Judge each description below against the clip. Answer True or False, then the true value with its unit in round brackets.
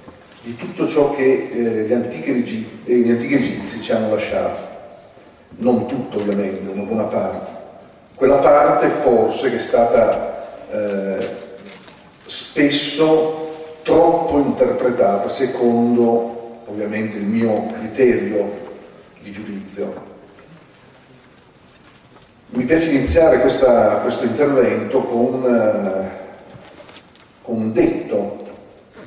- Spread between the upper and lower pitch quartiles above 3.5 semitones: True (4.0 semitones)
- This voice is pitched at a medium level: False (120 Hz)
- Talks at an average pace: False (95 wpm)